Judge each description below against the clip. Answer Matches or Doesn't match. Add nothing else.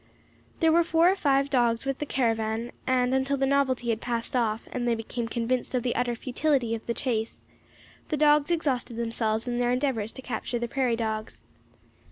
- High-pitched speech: Matches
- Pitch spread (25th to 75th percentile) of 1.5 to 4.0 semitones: Matches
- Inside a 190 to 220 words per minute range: Matches